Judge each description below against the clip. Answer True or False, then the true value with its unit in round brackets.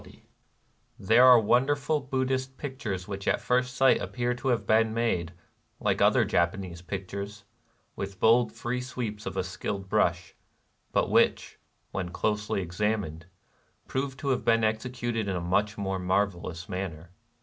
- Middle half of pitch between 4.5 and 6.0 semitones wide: True (4.8 semitones)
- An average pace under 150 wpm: False (155 wpm)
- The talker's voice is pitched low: True (105 Hz)